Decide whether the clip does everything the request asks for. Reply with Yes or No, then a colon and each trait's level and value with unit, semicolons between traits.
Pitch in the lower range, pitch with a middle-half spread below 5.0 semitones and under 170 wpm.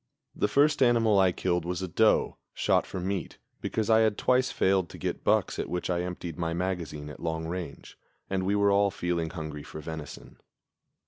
No: very low, 90 Hz; average, 3.3 semitones; average, 195 wpm